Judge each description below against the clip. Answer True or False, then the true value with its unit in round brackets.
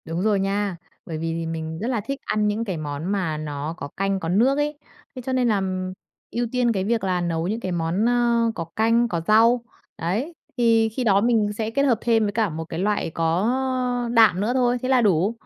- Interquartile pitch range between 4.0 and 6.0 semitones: True (5.3 semitones)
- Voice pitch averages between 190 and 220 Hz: True (210 Hz)